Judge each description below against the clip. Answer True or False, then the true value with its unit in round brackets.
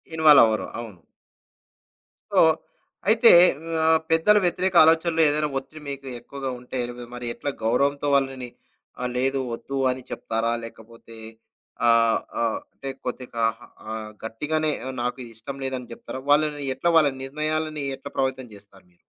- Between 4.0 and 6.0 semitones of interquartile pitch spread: True (4.6 semitones)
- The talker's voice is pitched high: False (135 Hz)